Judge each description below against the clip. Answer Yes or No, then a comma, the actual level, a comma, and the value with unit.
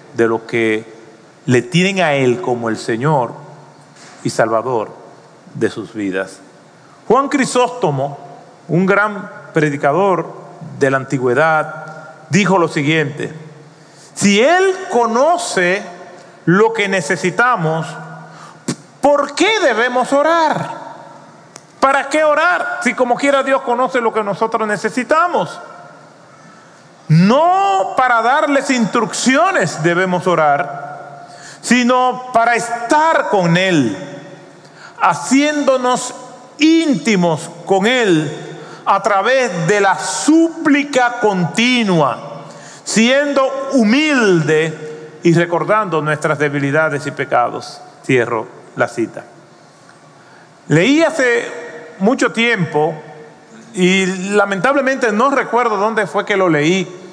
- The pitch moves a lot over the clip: Yes, wide, 8.1 semitones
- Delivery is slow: Yes, slow, 100 wpm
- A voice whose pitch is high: Yes, high, 195 Hz